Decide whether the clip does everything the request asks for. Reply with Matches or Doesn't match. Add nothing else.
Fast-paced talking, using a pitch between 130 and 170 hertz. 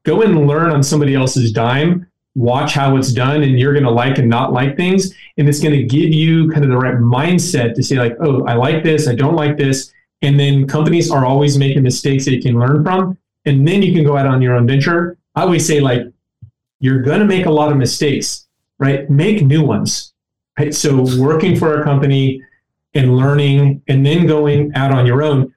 Matches